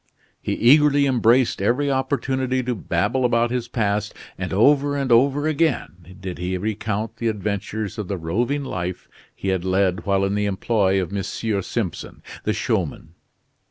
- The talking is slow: No, average, 160 wpm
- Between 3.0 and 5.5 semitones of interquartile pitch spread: Yes, average, 5.2 semitones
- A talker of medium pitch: No, low, 110 Hz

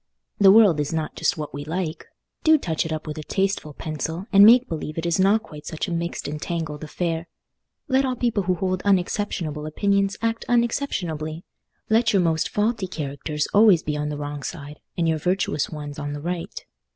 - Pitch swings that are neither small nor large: Yes, average, 4.7 semitones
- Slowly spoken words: No, average, 195 wpm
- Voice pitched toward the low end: No, medium, 170 Hz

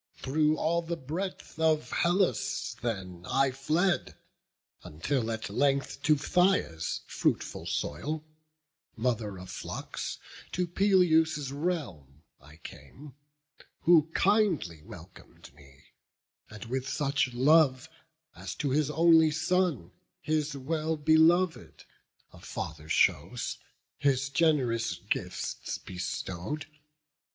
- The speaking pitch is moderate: Yes, medium, 145 Hz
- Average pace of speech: No, slow, 105 wpm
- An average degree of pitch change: No, wide, 5.8 semitones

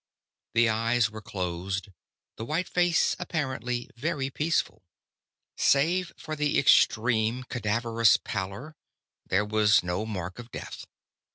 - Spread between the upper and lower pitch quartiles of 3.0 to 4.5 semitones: No, average, 5.2 semitones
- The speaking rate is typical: No, slow, 115 wpm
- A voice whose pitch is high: No, low, 115 Hz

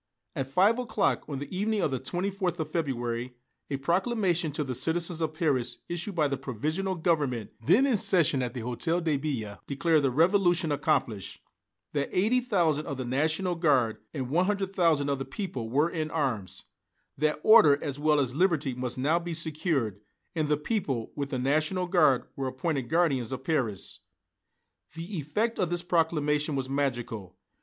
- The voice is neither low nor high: Yes, medium, 150 Hz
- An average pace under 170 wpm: No, average, 175 wpm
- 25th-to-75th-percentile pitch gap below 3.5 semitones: No, average, 4.7 semitones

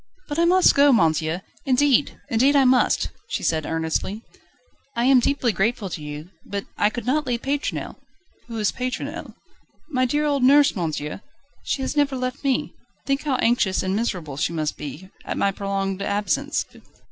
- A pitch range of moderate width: No, wide, 6.4 semitones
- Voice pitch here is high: Yes, high, 235 Hz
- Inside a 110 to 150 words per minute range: No, average, 170 wpm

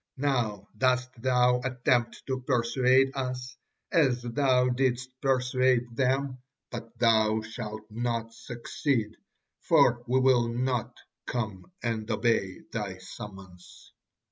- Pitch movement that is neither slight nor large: No, narrow, 2.2 semitones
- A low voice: Yes, low, 120 Hz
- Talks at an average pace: No, slow, 110 wpm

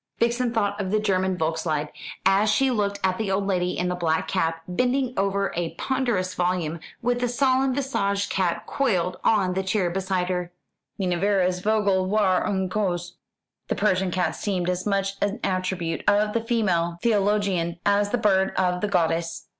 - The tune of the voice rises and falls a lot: No, average, 2.7 semitones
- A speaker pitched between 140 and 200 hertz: Yes, high, 190 Hz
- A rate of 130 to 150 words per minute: No, average, 170 wpm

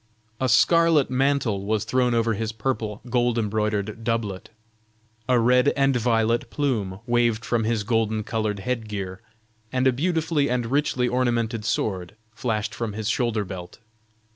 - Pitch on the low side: Yes, low, 115 Hz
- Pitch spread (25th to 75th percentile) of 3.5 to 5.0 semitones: No, average, 2.9 semitones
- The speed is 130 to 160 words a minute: Yes, average, 145 wpm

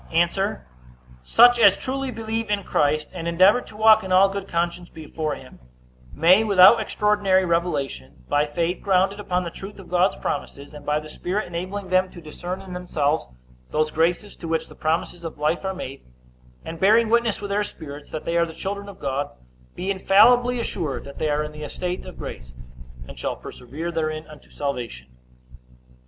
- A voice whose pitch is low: No, medium, 175 Hz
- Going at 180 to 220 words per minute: Yes, average, 185 wpm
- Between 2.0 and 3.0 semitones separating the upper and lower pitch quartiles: No, average, 4.5 semitones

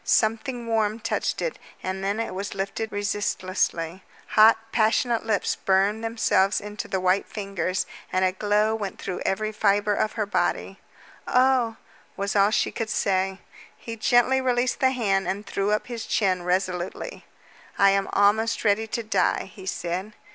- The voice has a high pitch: Yes, high, 205 Hz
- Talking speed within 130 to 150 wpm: No, average, 160 wpm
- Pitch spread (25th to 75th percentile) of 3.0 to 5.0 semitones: No, narrow, 2.6 semitones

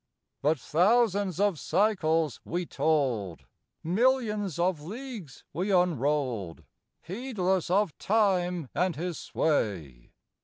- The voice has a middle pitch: Yes, medium, 175 Hz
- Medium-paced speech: No, slow, 100 wpm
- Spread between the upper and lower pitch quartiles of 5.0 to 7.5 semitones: Yes, average, 5.3 semitones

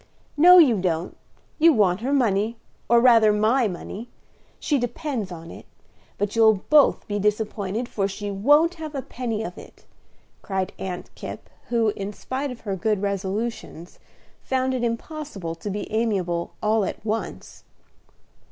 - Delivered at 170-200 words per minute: No, average, 150 wpm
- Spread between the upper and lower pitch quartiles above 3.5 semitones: Yes, average, 4.3 semitones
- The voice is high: Yes, high, 220 Hz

